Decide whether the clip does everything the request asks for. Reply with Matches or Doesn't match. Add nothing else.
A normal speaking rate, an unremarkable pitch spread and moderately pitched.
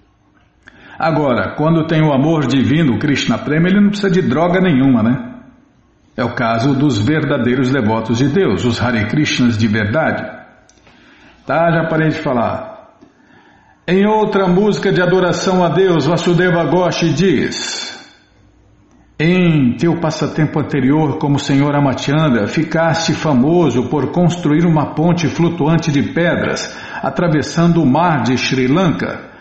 Matches